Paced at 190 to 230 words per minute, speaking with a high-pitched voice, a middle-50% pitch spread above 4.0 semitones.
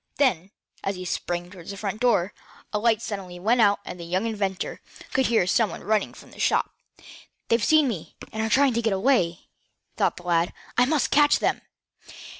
Yes: average, 200 wpm; high, 210 Hz; average, 4.6 semitones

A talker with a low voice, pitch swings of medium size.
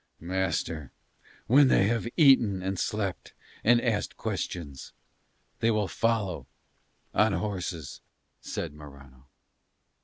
No: very low, 95 Hz; wide, 5.8 semitones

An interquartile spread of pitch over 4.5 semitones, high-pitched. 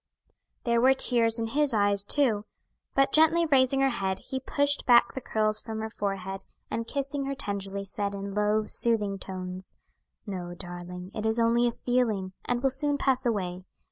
Yes: average, 4.9 semitones; high, 220 Hz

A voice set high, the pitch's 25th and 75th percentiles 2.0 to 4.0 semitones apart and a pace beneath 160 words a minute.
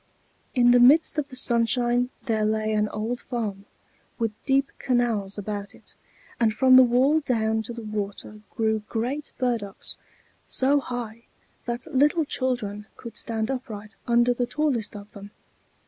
Yes: high, 235 Hz; average, 2.9 semitones; average, 150 wpm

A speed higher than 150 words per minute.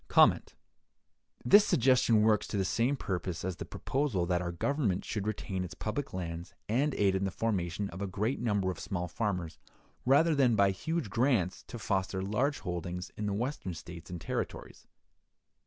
Yes: average, 170 wpm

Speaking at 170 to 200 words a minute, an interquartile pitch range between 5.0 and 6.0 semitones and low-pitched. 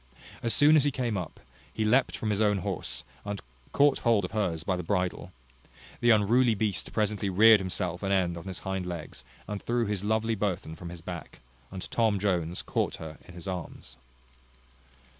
No: average, 185 wpm; average, 3.6 semitones; low, 100 Hz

